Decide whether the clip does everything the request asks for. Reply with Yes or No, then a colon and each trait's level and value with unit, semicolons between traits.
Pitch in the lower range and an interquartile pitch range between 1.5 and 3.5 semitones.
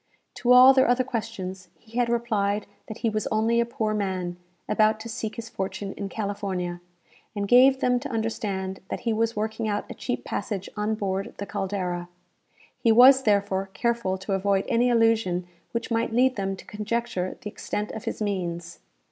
No: high, 215 Hz; average, 3.2 semitones